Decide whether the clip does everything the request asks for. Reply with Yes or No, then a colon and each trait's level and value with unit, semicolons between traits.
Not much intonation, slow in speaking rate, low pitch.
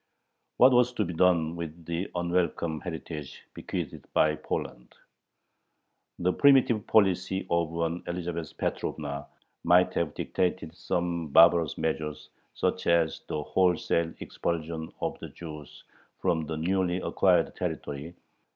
Yes: narrow, 2.2 semitones; slow, 125 wpm; very low, 85 Hz